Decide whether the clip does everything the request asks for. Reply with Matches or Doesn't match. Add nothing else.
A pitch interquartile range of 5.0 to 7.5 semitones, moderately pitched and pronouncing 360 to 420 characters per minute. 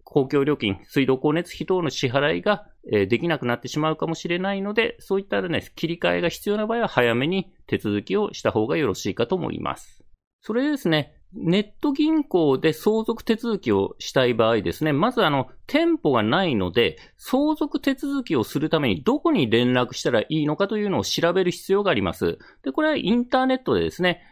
Doesn't match